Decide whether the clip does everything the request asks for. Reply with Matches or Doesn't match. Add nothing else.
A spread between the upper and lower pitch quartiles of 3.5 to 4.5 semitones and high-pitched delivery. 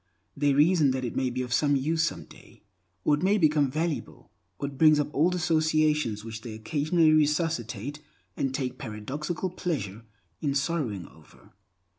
Doesn't match